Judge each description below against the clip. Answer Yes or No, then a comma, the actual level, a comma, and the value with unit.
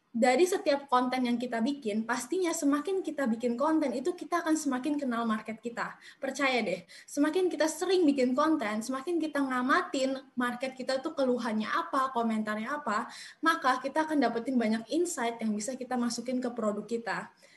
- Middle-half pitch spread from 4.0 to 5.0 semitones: Yes, average, 4.3 semitones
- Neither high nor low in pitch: No, very high, 265 Hz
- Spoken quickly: Yes, fast, 165 wpm